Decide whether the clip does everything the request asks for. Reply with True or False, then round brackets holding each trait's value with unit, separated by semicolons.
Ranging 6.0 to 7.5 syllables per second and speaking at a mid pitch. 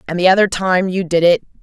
True (6.2 syllables/s; 180 Hz)